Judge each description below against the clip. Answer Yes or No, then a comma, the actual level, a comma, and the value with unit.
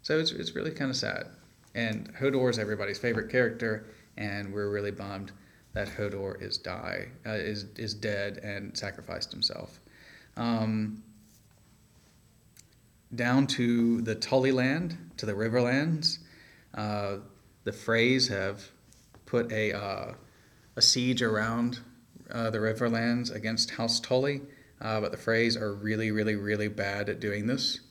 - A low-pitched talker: Yes, low, 110 Hz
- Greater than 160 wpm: No, average, 140 wpm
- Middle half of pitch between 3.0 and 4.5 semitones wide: No, narrow, 2.6 semitones